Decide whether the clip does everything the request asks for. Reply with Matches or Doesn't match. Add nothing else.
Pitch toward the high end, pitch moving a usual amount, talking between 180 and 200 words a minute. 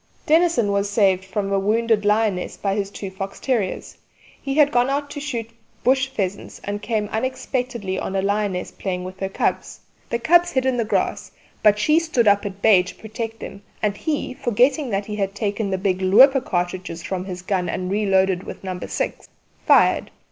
Matches